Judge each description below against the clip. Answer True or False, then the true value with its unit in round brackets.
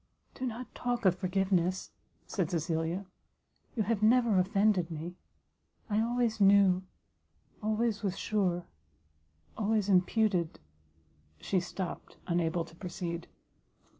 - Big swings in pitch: False (3.8 semitones)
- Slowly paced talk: True (110 wpm)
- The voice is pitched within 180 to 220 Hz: True (190 Hz)